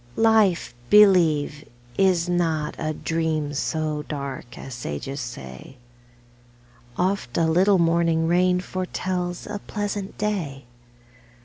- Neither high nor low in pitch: Yes, medium, 165 Hz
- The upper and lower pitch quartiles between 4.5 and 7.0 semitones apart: No, average, 4.1 semitones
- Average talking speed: No, slow, 110 wpm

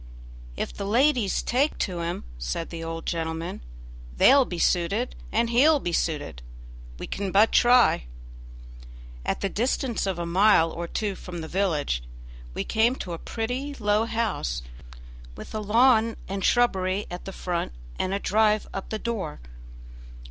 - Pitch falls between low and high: No, high, 200 Hz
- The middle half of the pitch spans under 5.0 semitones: No, average, 5.3 semitones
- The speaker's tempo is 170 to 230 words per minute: No, average, 160 wpm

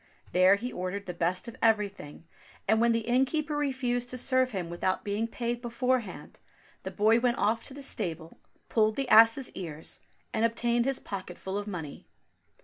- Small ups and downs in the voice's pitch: No, average, 4.4 semitones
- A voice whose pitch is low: No, high, 225 Hz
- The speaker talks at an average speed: Yes, average, 175 wpm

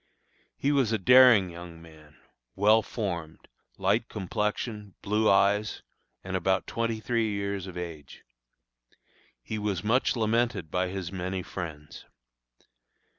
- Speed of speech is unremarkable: No, slow, 125 wpm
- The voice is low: Yes, low, 100 Hz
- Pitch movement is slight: No, average, 3.7 semitones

